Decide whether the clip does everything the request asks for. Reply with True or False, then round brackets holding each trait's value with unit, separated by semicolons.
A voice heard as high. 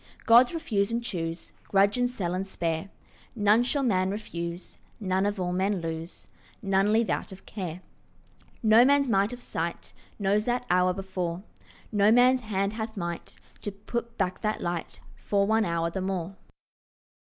True (200 Hz)